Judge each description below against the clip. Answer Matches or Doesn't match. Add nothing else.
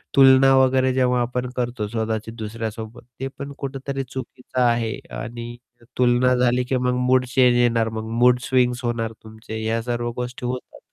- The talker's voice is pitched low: Matches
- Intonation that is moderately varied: Doesn't match